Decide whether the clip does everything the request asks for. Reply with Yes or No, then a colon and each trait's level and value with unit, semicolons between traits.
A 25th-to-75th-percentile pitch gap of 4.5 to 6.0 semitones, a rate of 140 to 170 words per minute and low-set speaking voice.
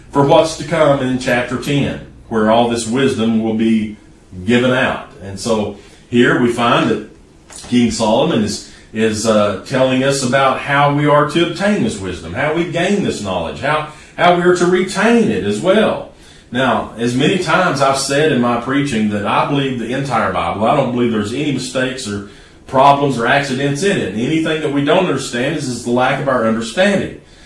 No: average, 4.8 semitones; average, 195 wpm; low, 130 Hz